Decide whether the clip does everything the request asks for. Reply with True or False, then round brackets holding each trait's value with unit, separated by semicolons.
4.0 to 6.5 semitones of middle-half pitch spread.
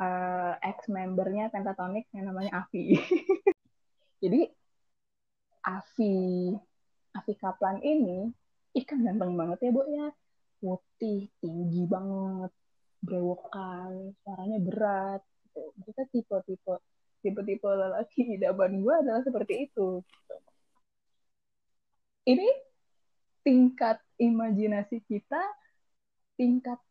True (4.6 semitones)